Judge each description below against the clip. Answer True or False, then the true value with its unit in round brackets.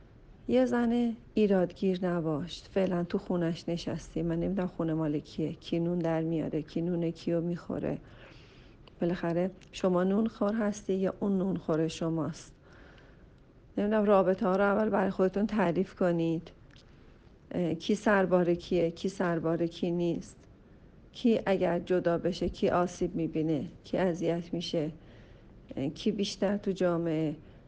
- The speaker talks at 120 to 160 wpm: True (130 wpm)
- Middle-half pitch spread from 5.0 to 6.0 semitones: False (2.7 semitones)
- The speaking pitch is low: False (175 Hz)